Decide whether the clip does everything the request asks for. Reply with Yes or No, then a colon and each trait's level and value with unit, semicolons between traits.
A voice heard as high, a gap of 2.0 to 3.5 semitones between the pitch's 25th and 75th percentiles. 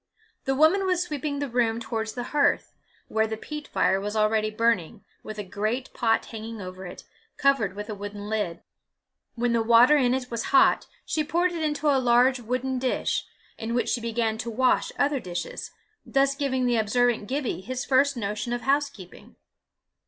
No: high, 240 Hz; average, 3.9 semitones